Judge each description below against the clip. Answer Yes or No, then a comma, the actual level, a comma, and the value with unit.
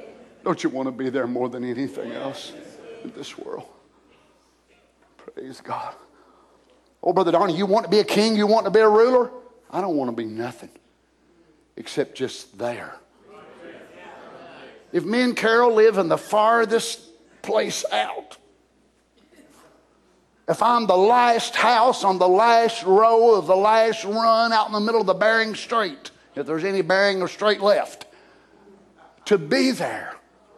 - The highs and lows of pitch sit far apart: No, average, 4.1 semitones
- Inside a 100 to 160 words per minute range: Yes, average, 155 wpm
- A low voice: No, high, 210 Hz